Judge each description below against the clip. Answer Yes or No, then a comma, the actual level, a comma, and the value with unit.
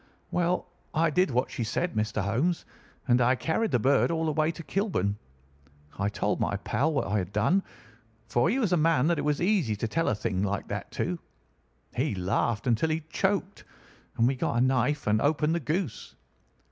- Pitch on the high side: No, medium, 140 Hz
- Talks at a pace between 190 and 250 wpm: Yes, average, 200 wpm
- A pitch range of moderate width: No, wide, 7.1 semitones